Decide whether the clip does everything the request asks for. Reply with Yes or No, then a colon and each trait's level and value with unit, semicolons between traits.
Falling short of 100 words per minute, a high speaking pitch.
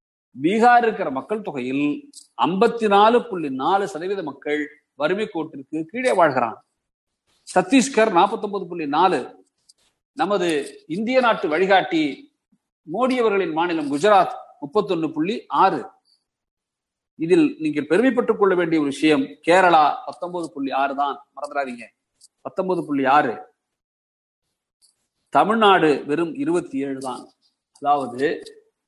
No: average, 110 wpm; high, 195 Hz